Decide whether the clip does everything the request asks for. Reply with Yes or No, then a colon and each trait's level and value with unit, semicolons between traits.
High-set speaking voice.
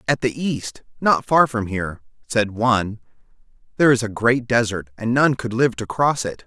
No: low, 120 Hz